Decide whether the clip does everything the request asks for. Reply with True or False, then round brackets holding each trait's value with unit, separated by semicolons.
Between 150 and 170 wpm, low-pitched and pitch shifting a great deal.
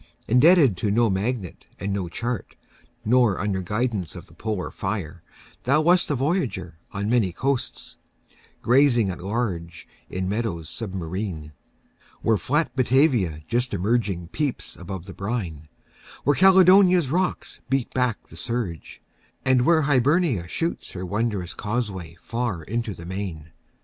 False (135 wpm; 110 Hz; 5.7 semitones)